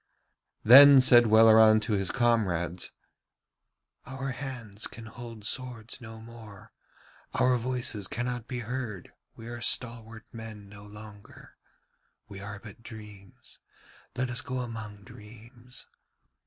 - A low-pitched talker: Yes, low, 115 Hz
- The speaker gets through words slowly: Yes, slow, 120 wpm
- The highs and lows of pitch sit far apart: No, average, 2.7 semitones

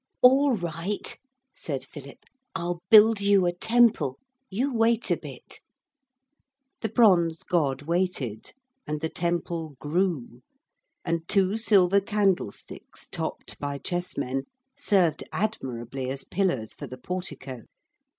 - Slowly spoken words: Yes, slow, 115 wpm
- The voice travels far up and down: Yes, wide, 6.0 semitones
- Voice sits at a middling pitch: Yes, medium, 175 Hz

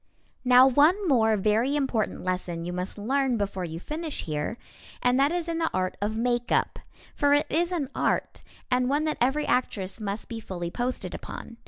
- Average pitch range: No, wide, 6.1 semitones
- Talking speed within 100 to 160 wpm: No, average, 185 wpm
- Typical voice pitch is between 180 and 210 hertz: No, high, 245 Hz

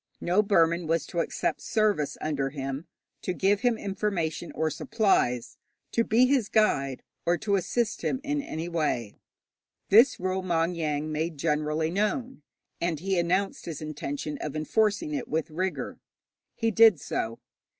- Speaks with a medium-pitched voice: Yes, medium, 175 Hz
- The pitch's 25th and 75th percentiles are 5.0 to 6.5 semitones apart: Yes, wide, 5.5 semitones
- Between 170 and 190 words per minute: No, average, 150 wpm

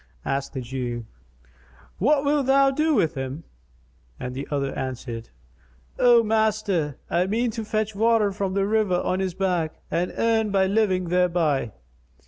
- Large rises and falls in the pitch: Yes, wide, 6.9 semitones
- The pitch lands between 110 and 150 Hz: No, high, 190 Hz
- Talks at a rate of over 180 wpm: No, average, 150 wpm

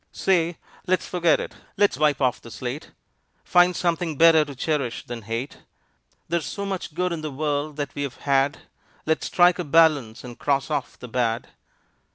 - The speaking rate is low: No, average, 175 wpm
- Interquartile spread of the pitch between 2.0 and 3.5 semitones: No, average, 4.2 semitones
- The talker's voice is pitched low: No, medium, 150 Hz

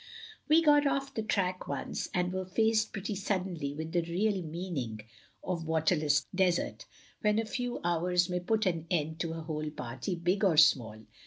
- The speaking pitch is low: No, medium, 180 Hz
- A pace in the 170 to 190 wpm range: Yes, average, 185 wpm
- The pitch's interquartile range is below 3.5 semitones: No, average, 4.3 semitones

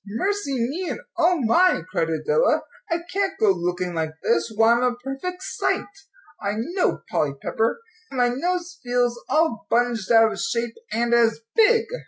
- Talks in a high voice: Yes, high, 245 Hz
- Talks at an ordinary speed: Yes, average, 170 wpm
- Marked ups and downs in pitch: Yes, wide, 7.6 semitones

